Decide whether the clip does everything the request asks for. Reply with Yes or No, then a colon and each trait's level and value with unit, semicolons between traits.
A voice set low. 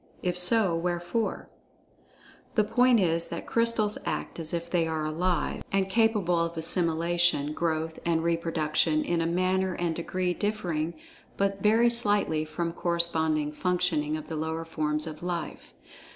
No: medium, 170 Hz